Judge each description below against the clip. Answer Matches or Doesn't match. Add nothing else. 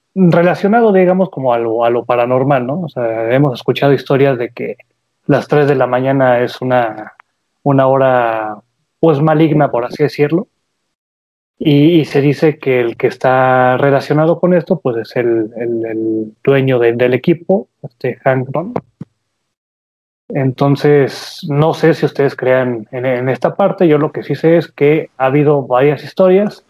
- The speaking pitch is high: Doesn't match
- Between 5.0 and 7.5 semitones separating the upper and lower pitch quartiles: Doesn't match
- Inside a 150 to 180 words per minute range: Matches